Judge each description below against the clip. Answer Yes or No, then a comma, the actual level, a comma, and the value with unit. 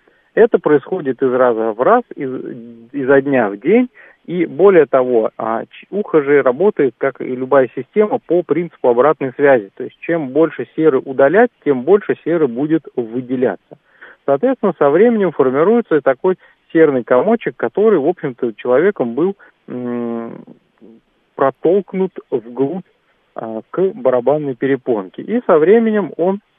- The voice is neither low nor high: Yes, medium, 150 Hz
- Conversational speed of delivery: Yes, average, 130 wpm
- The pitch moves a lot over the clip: Yes, wide, 7.3 semitones